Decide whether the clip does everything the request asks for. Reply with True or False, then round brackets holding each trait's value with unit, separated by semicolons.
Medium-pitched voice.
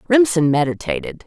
True (180 Hz)